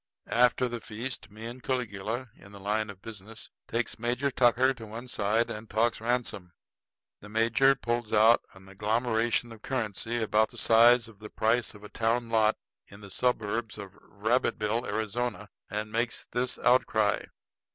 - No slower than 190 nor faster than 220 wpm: No, average, 160 wpm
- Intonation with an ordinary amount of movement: No, narrow, 2.2 semitones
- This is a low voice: Yes, low, 115 Hz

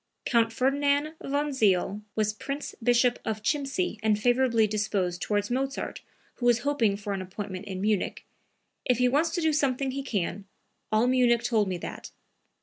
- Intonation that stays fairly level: No, average, 4.6 semitones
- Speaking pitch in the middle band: No, high, 235 Hz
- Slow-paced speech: No, average, 165 wpm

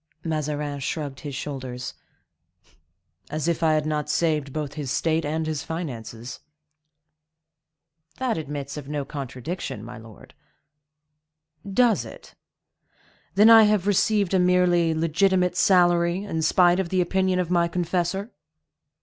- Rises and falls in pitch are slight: No, average, 3.7 semitones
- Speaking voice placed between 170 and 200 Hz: No, medium, 160 Hz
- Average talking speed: No, slow, 130 wpm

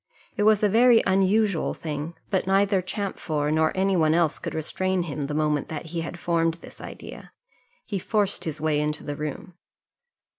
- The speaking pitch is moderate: Yes, medium, 170 Hz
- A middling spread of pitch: Yes, average, 4.1 semitones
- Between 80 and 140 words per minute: No, average, 180 wpm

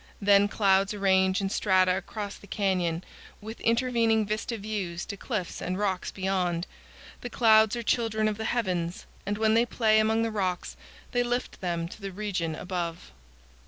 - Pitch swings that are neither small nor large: Yes, average, 3.0 semitones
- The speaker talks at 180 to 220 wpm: No, average, 165 wpm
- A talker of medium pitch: No, high, 200 Hz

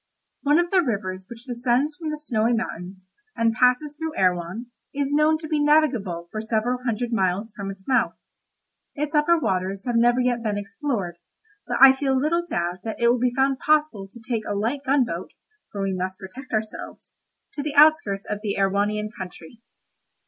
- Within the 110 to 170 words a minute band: No, average, 185 wpm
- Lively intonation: Yes, wide, 6.2 semitones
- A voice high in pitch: Yes, high, 235 Hz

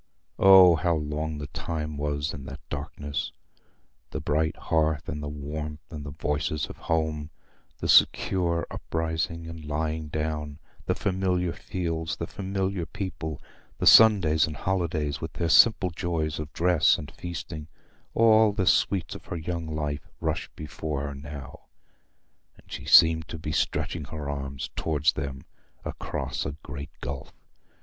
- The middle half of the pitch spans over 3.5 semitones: No, narrow, 2.4 semitones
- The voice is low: Yes, very low, 80 Hz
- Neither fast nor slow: Yes, average, 145 wpm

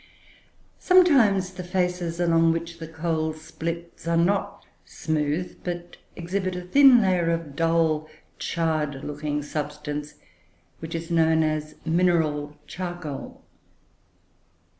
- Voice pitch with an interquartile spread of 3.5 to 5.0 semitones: No, narrow, 2.4 semitones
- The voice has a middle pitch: Yes, medium, 165 Hz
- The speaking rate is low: Yes, slow, 110 wpm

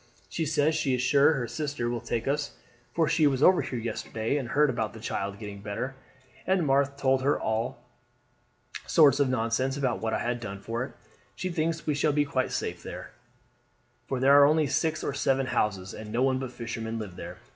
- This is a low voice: Yes, low, 130 Hz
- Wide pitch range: No, average, 4.1 semitones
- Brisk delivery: Yes, fast, 210 wpm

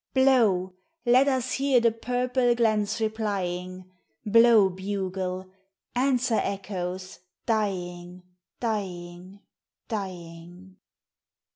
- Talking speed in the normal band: No, slow, 80 wpm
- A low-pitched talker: No, high, 200 Hz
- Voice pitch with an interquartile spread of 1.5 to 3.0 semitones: No, average, 4.3 semitones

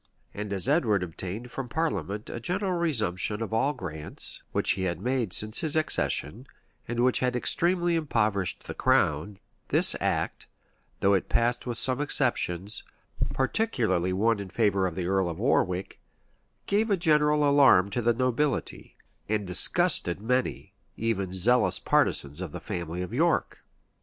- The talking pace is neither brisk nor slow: Yes, average, 150 wpm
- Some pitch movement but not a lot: No, wide, 6.1 semitones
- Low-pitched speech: Yes, low, 115 Hz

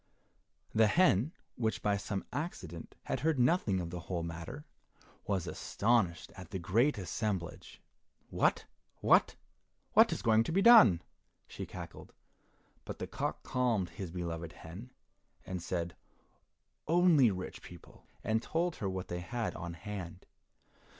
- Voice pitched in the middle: No, low, 100 Hz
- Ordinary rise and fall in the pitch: No, wide, 5.8 semitones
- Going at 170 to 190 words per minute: No, average, 140 wpm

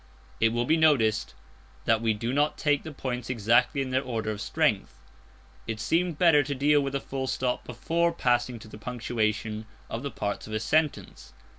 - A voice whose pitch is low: Yes, low, 125 Hz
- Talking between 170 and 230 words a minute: Yes, average, 190 wpm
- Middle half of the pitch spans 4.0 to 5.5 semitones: Yes, average, 4.5 semitones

